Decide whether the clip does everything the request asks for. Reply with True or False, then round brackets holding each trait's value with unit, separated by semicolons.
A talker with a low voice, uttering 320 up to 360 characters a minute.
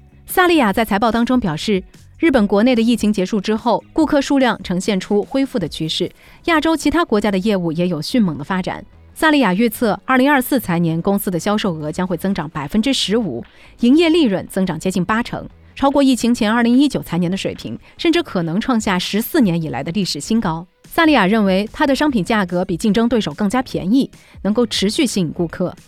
False (210 Hz; 330 characters per minute)